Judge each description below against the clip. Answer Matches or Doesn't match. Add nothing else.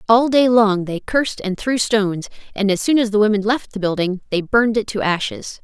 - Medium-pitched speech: Doesn't match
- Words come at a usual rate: Doesn't match